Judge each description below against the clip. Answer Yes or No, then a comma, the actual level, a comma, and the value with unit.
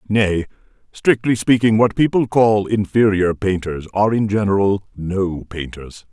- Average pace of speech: No, slow, 125 wpm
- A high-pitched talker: No, low, 100 Hz